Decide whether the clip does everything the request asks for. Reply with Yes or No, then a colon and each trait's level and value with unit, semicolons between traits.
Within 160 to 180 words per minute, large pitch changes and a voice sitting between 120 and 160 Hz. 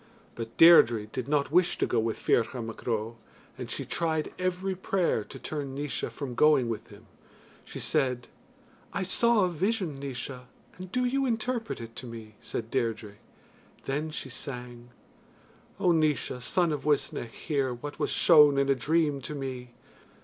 Yes: average, 165 wpm; wide, 5.7 semitones; medium, 140 Hz